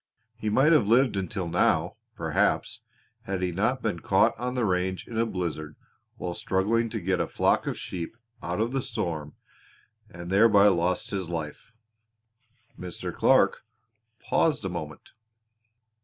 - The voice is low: Yes, very low, 95 Hz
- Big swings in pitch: No, average, 4.5 semitones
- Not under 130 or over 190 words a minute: Yes, average, 150 wpm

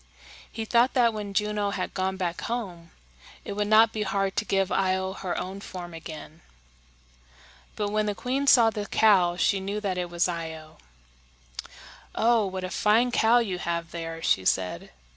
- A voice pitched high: Yes, high, 195 Hz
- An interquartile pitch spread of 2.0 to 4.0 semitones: Yes, average, 3.5 semitones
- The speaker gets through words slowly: No, average, 175 wpm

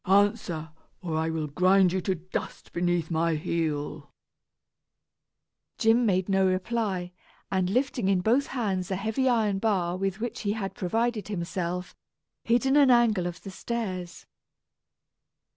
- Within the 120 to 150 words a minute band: Yes, average, 145 wpm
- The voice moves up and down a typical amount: Yes, average, 4.0 semitones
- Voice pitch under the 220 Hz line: Yes, high, 190 Hz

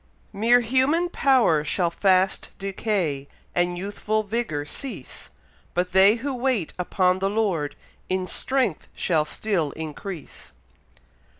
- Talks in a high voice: Yes, high, 195 Hz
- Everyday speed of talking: No, slow, 115 wpm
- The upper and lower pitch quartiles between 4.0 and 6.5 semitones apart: Yes, average, 4.8 semitones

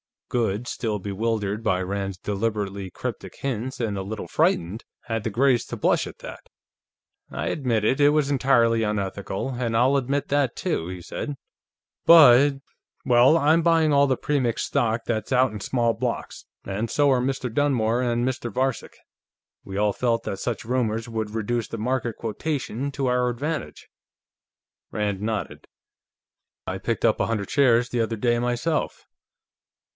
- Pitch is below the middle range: Yes, low, 120 Hz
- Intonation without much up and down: No, average, 3.6 semitones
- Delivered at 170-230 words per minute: No, average, 160 wpm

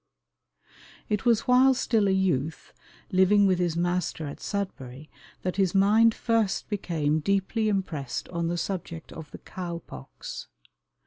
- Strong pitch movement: No, average, 3.8 semitones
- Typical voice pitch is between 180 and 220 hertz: Yes, medium, 185 Hz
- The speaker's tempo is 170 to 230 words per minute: No, average, 140 wpm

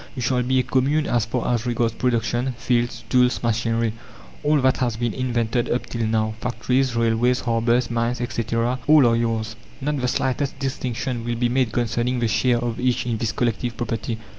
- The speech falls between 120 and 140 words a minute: No, average, 190 wpm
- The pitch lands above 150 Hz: No, low, 120 Hz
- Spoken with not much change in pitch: Yes, narrow, 1.6 semitones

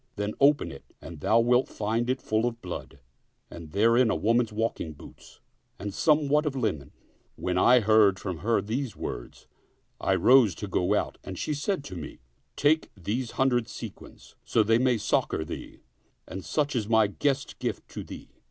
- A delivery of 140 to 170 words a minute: No, average, 180 wpm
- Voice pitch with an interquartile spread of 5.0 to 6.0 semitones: No, average, 4.5 semitones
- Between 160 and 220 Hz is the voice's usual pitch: No, low, 115 Hz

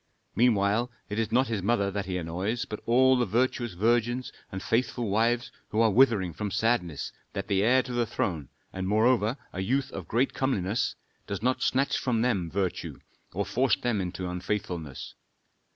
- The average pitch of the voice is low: Yes, low, 110 Hz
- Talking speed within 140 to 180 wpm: Yes, average, 175 wpm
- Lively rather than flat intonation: No, average, 4.2 semitones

